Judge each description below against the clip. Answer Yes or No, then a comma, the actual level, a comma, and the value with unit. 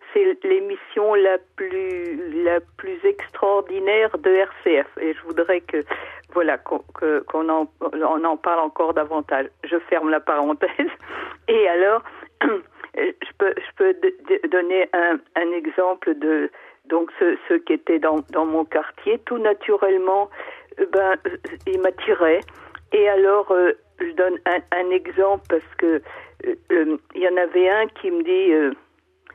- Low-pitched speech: No, high, 195 Hz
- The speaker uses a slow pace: Yes, slow, 135 wpm